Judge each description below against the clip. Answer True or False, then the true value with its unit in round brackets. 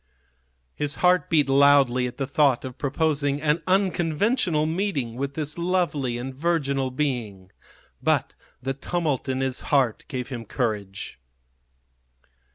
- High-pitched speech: False (140 Hz)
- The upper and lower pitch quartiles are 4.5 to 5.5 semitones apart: False (3.6 semitones)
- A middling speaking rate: False (130 wpm)